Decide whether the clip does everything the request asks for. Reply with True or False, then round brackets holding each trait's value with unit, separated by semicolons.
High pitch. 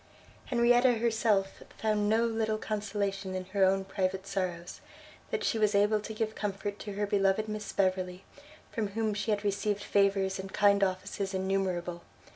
True (200 Hz)